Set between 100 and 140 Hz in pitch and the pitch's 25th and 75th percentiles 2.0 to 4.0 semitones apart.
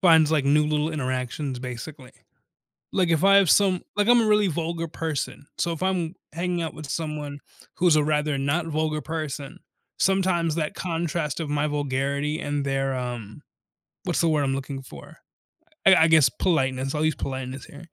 No: medium, 155 Hz; average, 3.3 semitones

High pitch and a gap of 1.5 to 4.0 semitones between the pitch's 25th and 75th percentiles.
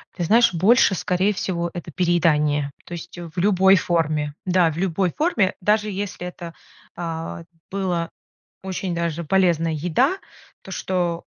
No: medium, 175 Hz; narrow, 2.4 semitones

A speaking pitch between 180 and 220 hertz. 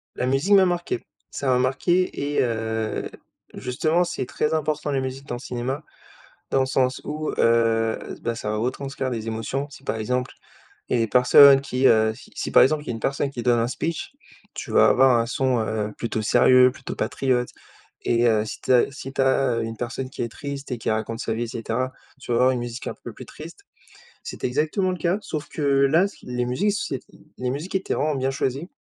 No: low, 130 Hz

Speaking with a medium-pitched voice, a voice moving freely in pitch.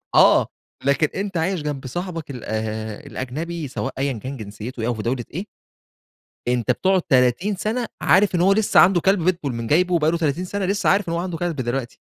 Yes: medium, 160 Hz; wide, 6.5 semitones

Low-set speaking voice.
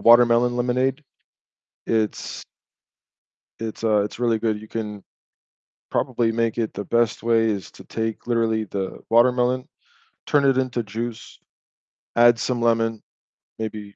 Yes: low, 115 Hz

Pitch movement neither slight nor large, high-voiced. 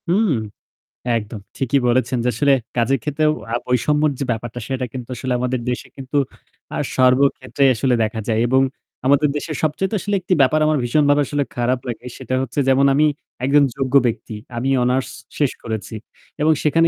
No: average, 3.3 semitones; low, 130 Hz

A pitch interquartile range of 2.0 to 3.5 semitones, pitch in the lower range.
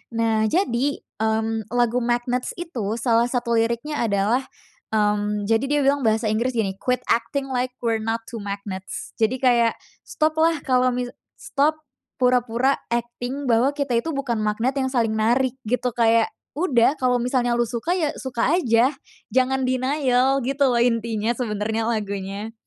No: average, 2.7 semitones; high, 240 Hz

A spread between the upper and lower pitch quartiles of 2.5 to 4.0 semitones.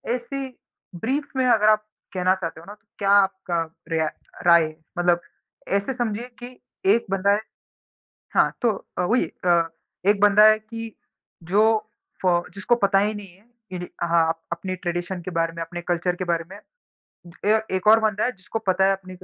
Yes: average, 3.7 semitones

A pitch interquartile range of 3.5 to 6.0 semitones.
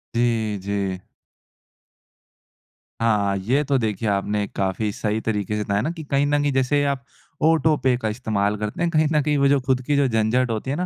Yes: average, 5.1 semitones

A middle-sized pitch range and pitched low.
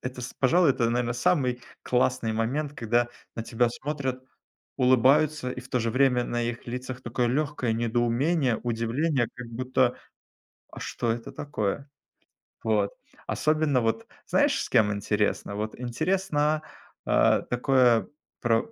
Yes: average, 3.2 semitones; low, 125 Hz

